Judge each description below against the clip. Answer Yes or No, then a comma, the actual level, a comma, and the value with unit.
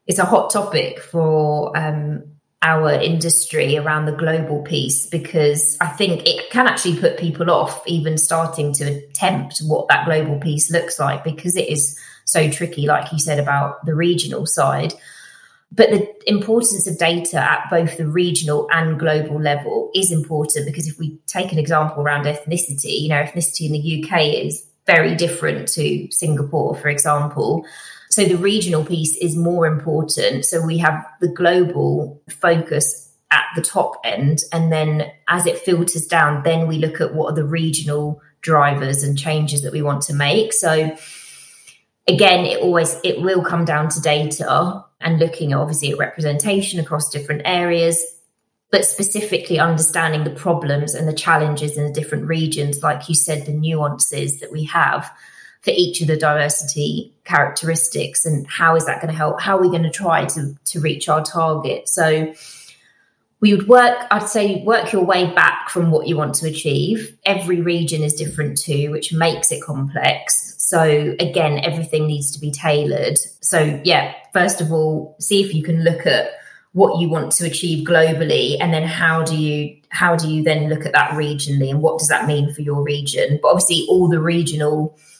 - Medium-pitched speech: Yes, medium, 160 Hz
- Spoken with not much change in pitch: Yes, narrow, 2.2 semitones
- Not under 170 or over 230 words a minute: Yes, average, 180 wpm